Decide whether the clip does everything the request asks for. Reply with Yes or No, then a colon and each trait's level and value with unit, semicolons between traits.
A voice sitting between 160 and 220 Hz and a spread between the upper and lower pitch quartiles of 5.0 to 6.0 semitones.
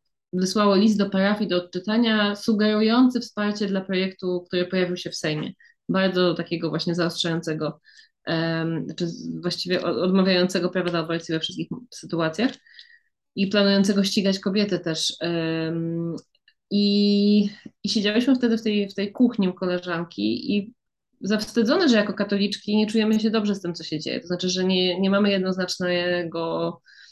No: high, 190 Hz; average, 3.5 semitones